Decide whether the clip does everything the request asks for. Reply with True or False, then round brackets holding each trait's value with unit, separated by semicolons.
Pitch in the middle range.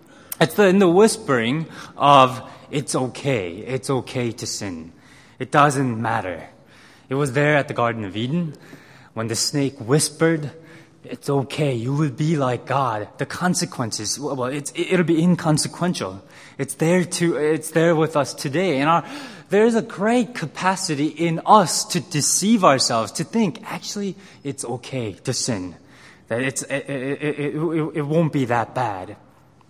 True (145 Hz)